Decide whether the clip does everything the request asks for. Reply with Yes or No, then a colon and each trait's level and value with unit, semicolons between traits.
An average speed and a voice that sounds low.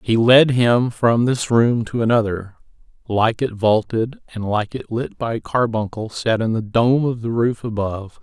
Yes: average, 180 wpm; low, 115 Hz